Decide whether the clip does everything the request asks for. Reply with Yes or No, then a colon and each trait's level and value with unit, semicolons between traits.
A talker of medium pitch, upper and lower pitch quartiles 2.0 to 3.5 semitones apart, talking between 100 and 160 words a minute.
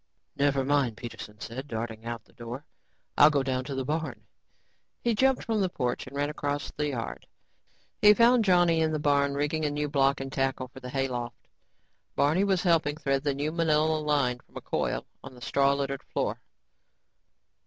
No: medium, 145 Hz; average, 2.9 semitones; average, 185 wpm